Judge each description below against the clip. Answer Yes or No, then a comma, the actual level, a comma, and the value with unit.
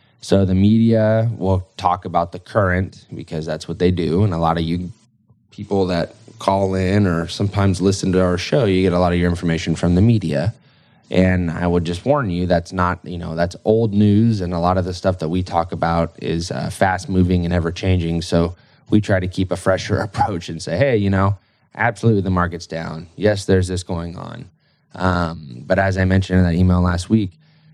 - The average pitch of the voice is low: Yes, very low, 90 Hz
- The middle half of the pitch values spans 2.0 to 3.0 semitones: Yes, average, 2.7 semitones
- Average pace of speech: No, fast, 215 wpm